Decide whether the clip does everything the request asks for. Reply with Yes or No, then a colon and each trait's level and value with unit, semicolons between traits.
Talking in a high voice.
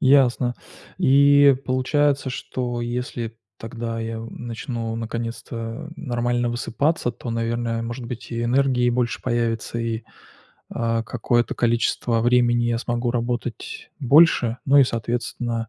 No: low, 120 Hz